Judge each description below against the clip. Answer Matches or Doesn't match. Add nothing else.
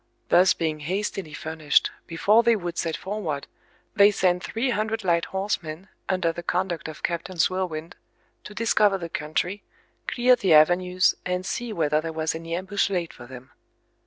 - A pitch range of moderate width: Matches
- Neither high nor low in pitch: Matches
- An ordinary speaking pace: Matches